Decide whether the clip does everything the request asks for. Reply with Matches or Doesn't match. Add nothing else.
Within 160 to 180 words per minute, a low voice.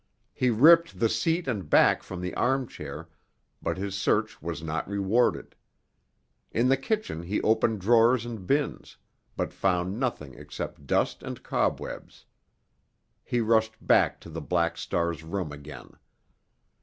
Doesn't match